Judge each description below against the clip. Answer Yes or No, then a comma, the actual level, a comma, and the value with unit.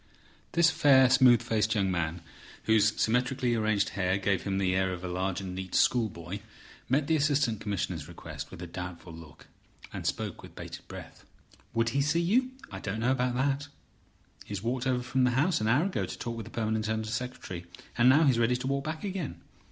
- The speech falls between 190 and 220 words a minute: Yes, fast, 205 wpm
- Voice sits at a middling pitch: No, low, 115 Hz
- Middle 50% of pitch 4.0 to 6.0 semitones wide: Yes, wide, 5.5 semitones